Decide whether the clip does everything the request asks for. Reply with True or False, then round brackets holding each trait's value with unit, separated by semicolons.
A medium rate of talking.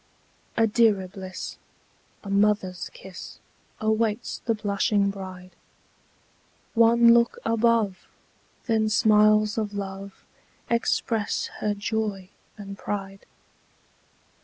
False (90 wpm)